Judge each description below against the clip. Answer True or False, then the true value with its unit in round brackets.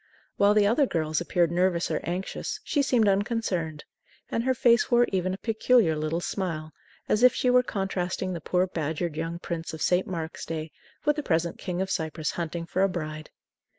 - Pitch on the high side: False (180 Hz)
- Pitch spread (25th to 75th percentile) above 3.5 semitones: True (4.3 semitones)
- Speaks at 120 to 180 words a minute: False (190 wpm)